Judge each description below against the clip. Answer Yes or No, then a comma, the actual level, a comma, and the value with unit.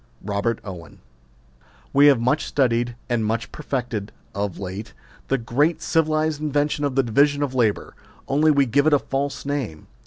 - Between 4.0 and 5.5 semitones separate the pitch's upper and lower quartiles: Yes, average, 4.3 semitones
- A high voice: No, low, 135 Hz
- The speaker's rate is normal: Yes, average, 160 wpm